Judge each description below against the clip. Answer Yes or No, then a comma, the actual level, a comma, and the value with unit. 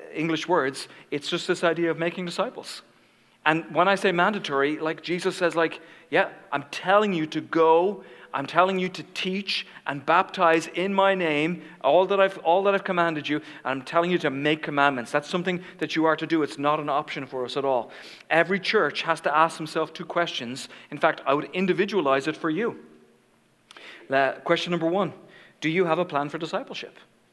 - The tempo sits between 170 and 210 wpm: Yes, average, 200 wpm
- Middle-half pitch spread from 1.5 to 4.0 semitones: Yes, average, 3.3 semitones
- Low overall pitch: No, medium, 165 Hz